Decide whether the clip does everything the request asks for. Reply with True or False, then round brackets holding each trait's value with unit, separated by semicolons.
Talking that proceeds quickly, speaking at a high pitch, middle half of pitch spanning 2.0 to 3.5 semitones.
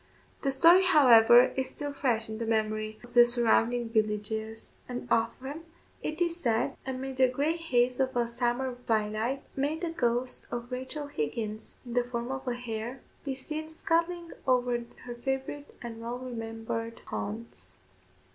False (155 wpm; 245 Hz; 2.9 semitones)